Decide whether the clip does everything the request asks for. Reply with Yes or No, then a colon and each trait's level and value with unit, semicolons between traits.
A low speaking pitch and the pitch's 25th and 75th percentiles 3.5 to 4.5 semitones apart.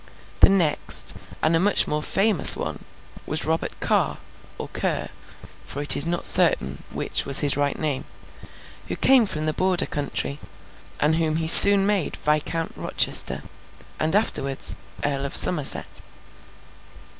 No: medium, 155 Hz; average, 3.8 semitones